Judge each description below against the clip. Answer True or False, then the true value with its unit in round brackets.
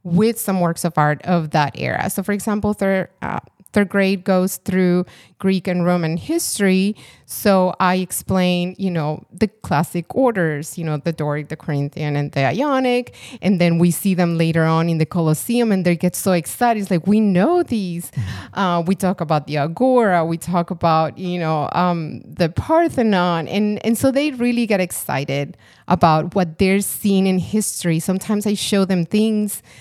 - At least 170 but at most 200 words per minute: True (180 wpm)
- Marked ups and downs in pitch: False (3.6 semitones)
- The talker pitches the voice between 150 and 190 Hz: True (185 Hz)